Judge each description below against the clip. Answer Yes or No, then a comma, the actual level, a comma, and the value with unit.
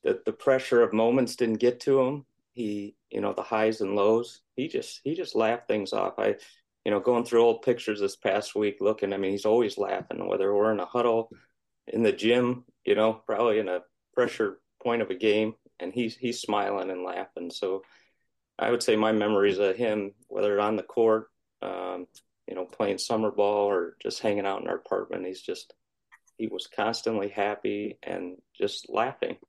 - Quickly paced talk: No, average, 195 wpm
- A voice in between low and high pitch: No, low, 110 Hz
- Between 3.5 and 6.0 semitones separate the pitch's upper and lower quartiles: No, average, 2.8 semitones